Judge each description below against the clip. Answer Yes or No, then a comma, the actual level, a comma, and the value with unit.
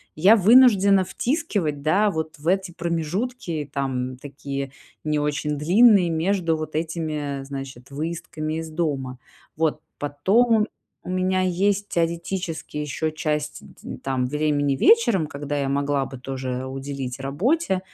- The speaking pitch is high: No, medium, 155 Hz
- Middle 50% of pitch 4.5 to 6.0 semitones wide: Yes, average, 4.8 semitones